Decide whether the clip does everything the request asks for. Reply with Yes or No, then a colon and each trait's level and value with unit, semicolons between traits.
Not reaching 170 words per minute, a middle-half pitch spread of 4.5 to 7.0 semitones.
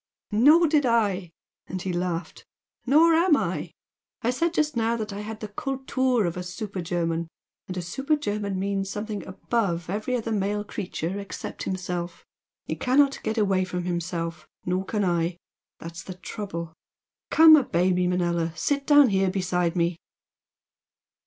Yes: average, 160 wpm; average, 4.8 semitones